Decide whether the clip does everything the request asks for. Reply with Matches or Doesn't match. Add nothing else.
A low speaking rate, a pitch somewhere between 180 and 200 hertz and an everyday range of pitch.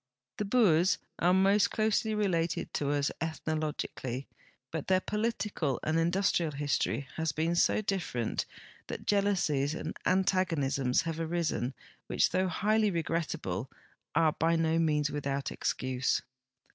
Doesn't match